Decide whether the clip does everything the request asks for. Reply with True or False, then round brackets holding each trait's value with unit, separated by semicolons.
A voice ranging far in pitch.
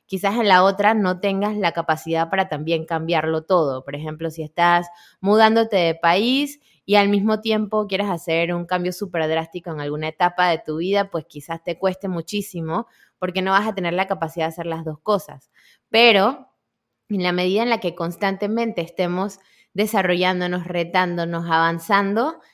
False (3.5 semitones)